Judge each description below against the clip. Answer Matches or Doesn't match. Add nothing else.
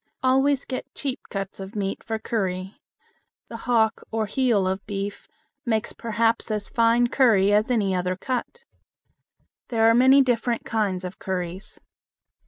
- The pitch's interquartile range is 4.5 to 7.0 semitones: Doesn't match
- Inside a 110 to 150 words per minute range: Matches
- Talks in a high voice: Matches